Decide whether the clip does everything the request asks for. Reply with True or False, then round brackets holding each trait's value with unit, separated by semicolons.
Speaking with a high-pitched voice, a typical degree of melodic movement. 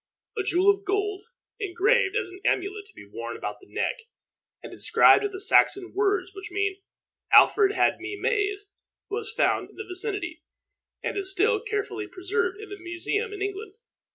False (400 Hz; 1.7 semitones)